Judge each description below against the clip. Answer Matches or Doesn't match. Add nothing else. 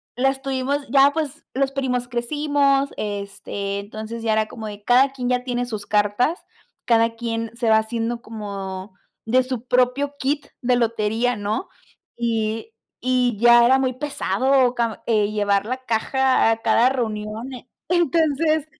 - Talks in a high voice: Matches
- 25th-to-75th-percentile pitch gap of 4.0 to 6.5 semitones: Doesn't match